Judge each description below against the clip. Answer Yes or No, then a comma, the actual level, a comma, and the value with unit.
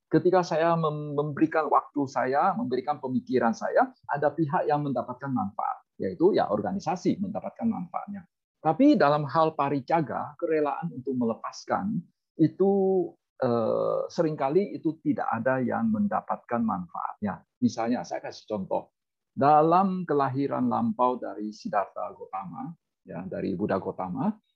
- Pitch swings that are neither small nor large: No, wide, 5.8 semitones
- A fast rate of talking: No, average, 115 wpm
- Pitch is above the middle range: No, medium, 160 Hz